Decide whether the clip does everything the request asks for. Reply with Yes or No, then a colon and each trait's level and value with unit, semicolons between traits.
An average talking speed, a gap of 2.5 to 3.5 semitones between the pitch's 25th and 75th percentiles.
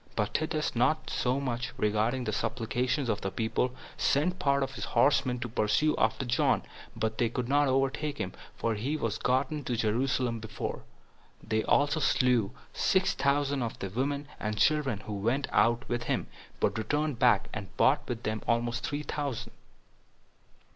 No: average, 170 wpm; average, 4.0 semitones